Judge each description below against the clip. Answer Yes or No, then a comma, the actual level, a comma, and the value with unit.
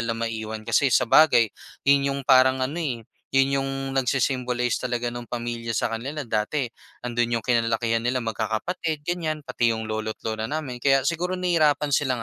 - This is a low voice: Yes, low, 125 Hz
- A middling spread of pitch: Yes, average, 3.4 semitones